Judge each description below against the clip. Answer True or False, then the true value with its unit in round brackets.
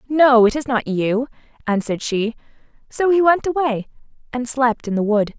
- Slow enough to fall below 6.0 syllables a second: True (5.0 syllables/s)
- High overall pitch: True (250 Hz)